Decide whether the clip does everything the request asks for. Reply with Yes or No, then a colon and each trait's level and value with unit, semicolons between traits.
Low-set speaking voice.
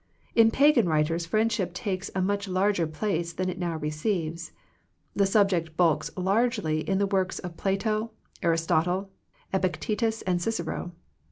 No: medium, 185 Hz